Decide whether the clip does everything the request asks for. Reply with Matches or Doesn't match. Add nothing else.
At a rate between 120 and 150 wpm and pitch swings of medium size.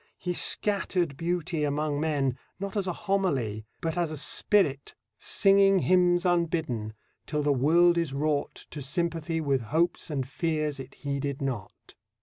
Matches